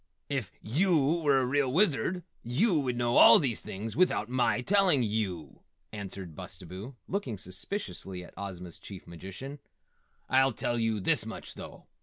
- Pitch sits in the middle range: No, low, 120 Hz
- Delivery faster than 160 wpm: No, average, 150 wpm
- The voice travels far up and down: Yes, wide, 6.6 semitones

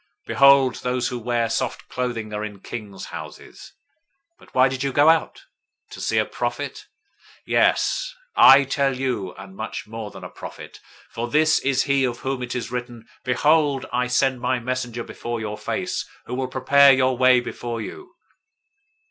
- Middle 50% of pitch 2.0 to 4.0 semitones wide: Yes, narrow, 2.5 semitones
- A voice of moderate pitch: No, low, 125 Hz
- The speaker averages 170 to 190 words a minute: Yes, average, 175 wpm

